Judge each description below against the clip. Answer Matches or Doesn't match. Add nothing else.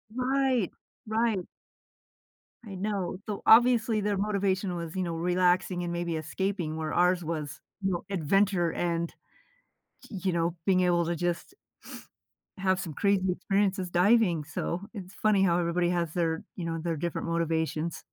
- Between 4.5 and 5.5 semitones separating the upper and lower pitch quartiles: Doesn't match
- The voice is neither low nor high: Matches